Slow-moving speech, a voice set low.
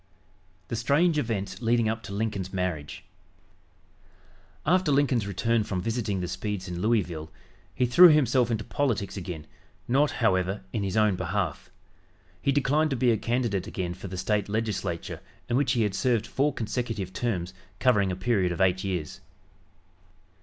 No: average, 160 wpm; low, 105 Hz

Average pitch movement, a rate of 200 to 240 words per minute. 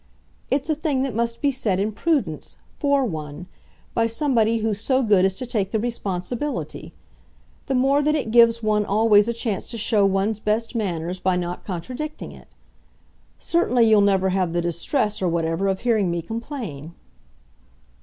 No: average, 4.6 semitones; average, 170 wpm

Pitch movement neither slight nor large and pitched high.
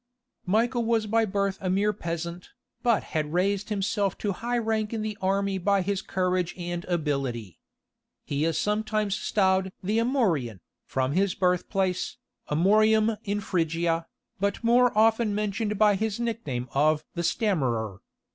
Yes: average, 4.0 semitones; high, 195 Hz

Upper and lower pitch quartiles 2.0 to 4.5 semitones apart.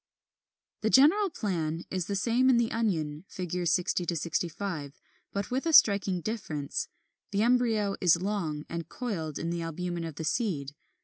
No: average, 5.2 semitones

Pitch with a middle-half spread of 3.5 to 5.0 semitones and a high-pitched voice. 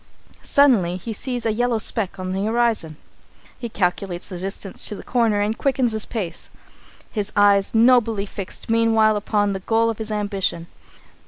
No: narrow, 2.6 semitones; high, 215 Hz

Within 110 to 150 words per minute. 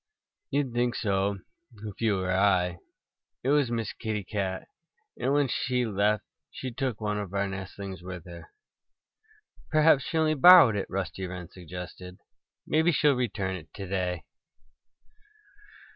Yes: average, 145 wpm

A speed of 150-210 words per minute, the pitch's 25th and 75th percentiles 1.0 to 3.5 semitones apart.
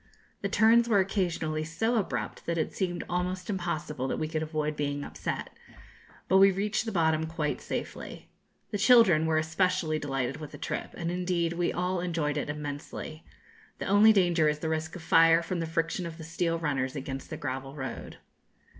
Yes: average, 185 wpm; average, 3.1 semitones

